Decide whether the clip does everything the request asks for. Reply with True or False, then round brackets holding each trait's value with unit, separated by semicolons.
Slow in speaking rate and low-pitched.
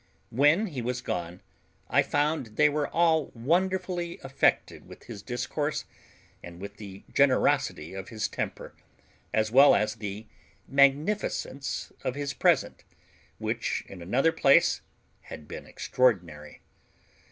True (125 wpm; 130 Hz)